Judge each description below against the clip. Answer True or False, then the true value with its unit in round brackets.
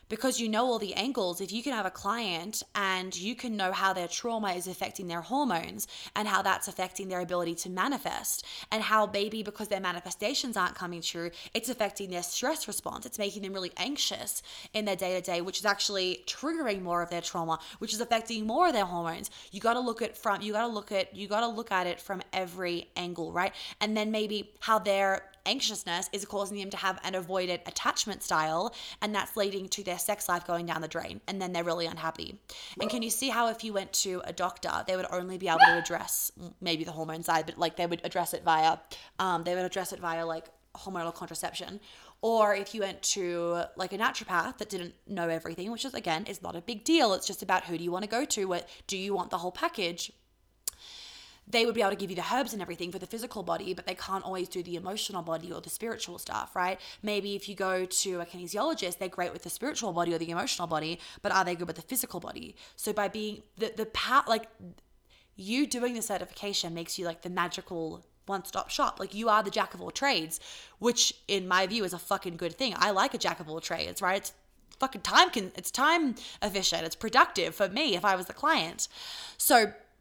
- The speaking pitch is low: False (195 Hz)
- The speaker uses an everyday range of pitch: True (3.6 semitones)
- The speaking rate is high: True (230 wpm)